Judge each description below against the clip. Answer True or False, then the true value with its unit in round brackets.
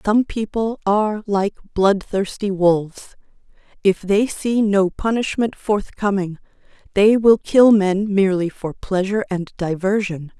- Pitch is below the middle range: False (200 Hz)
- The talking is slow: True (120 wpm)